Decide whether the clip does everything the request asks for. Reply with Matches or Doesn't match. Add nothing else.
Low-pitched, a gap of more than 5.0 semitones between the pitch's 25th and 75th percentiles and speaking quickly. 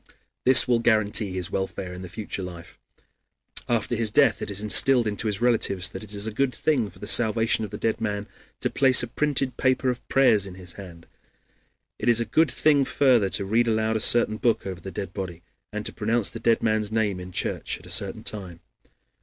Doesn't match